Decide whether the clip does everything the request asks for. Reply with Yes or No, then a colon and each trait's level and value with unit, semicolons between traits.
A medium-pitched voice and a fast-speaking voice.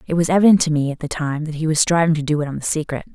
Yes: medium, 155 Hz; fast, 345 wpm